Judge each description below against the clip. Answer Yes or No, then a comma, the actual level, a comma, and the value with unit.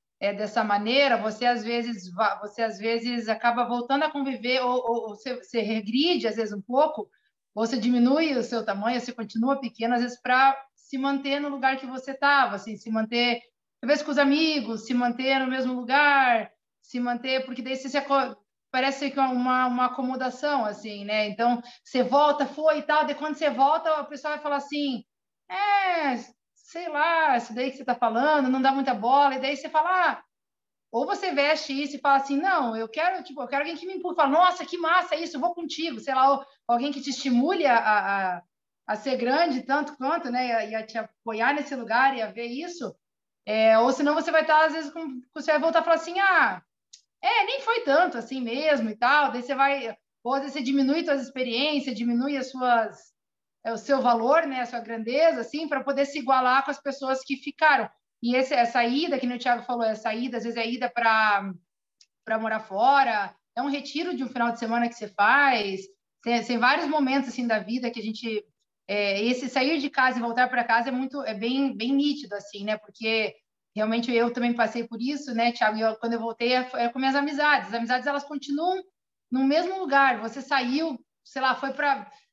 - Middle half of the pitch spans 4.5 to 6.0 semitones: No, average, 3.4 semitones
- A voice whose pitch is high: Yes, very high, 260 Hz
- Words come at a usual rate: No, fast, 215 wpm